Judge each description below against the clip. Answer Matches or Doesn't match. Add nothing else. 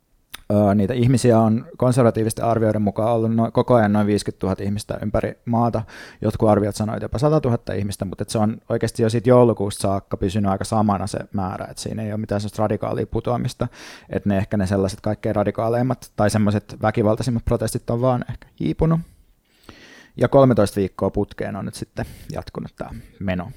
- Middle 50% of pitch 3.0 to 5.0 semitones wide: Doesn't match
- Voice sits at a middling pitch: Doesn't match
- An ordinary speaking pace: Doesn't match